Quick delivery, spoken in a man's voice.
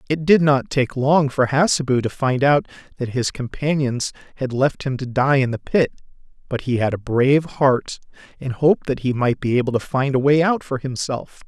Yes: fast, 215 wpm; male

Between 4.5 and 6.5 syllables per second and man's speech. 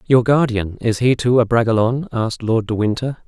Yes: 5.7 syllables/s; male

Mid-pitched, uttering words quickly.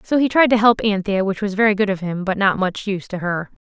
No: high, 200 Hz; fast, 290 wpm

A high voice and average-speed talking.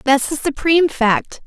Yes: very high, 285 Hz; average, 165 wpm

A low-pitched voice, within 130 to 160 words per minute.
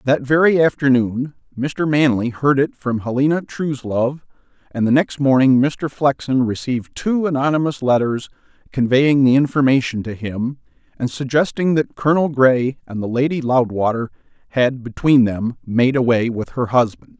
Yes: low, 130 Hz; average, 145 wpm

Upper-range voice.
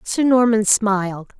Yes: high, 215 Hz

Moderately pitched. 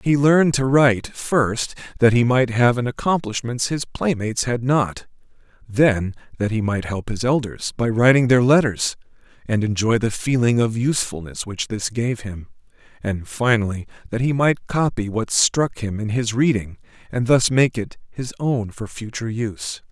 No: low, 120 Hz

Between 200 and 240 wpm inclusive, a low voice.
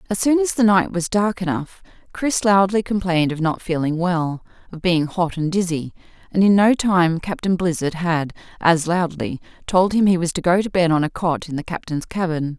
No: fast, 205 wpm; medium, 180 Hz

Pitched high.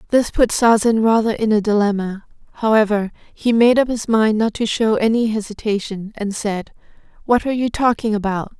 Yes: high, 220 Hz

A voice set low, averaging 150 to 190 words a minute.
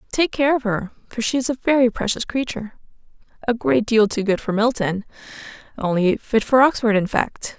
No: high, 230 Hz; average, 175 wpm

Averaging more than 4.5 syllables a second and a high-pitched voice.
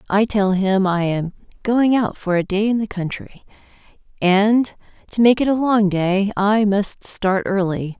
No: 4.1 syllables/s; high, 200 Hz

